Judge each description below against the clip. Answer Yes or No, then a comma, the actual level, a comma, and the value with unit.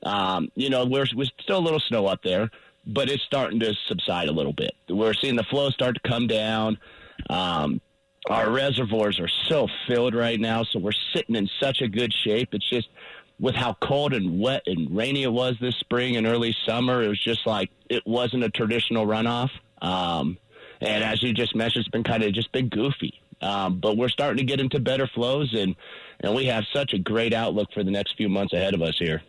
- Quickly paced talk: Yes, fast, 220 wpm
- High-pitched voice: No, low, 115 Hz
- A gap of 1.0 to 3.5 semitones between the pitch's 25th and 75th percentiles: Yes, average, 2.9 semitones